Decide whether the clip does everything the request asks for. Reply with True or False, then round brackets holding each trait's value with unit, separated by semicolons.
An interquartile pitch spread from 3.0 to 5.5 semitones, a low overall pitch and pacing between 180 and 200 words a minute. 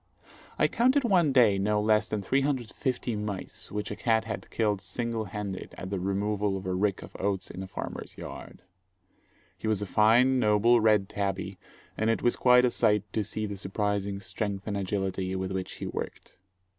False (2.6 semitones; 105 Hz; 185 wpm)